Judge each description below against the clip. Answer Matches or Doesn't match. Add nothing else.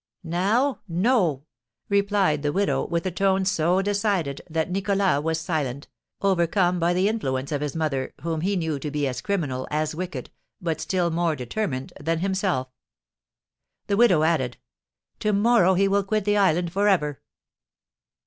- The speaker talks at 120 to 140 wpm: Doesn't match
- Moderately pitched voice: Matches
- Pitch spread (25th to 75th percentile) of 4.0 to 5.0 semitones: Matches